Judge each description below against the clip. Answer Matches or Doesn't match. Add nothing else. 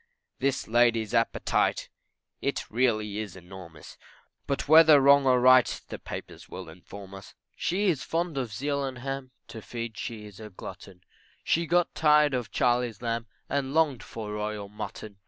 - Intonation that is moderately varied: Matches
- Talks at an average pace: Matches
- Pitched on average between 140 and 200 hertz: Doesn't match